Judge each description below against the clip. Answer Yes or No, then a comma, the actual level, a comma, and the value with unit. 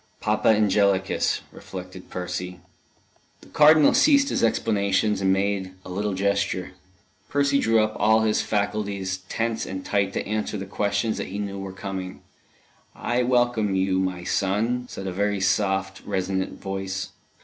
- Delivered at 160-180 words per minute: No, average, 150 wpm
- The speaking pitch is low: Yes, low, 100 Hz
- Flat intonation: Yes, narrow, 2.3 semitones